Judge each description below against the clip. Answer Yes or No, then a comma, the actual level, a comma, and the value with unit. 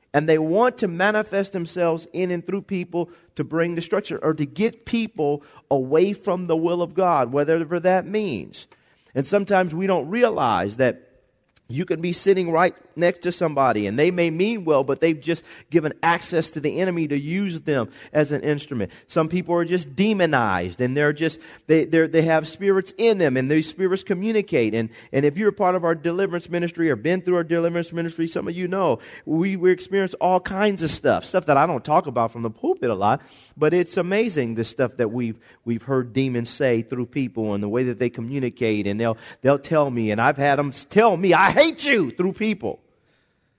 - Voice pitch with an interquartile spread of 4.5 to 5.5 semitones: Yes, average, 4.9 semitones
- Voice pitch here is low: No, medium, 165 Hz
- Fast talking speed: Yes, fast, 210 wpm